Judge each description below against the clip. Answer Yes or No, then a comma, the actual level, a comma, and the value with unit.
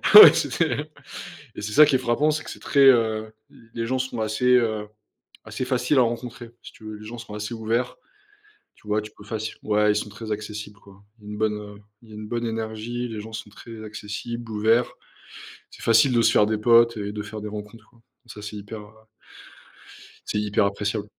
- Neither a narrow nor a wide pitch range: No, narrow, 2.0 semitones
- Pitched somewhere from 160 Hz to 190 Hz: No, low, 110 Hz